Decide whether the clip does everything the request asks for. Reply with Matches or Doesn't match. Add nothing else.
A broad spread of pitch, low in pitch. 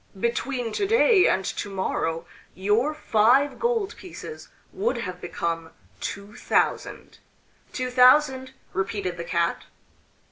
Doesn't match